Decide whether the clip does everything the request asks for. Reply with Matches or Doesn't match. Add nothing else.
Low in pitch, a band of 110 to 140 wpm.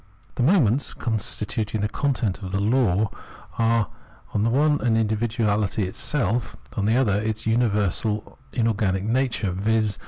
Matches